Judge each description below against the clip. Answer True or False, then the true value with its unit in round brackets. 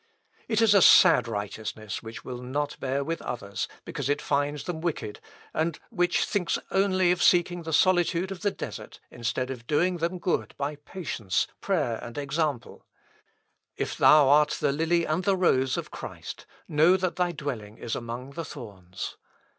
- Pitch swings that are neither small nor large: False (6.0 semitones)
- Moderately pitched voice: True (150 Hz)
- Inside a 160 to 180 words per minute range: True (170 wpm)